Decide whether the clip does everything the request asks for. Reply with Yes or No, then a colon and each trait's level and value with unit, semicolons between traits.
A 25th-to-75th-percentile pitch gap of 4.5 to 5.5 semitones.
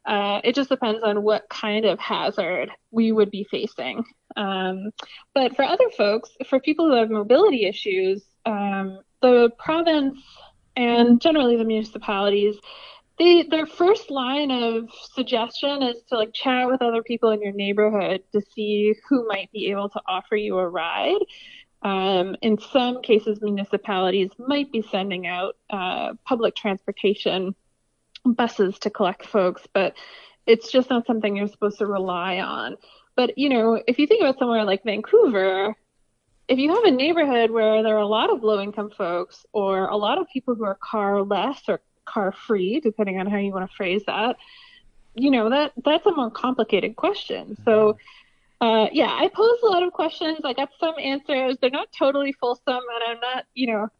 Yes: average, 4.8 semitones